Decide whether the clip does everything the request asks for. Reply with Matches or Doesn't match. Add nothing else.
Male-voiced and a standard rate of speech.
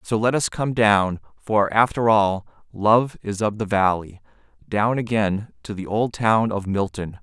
Matches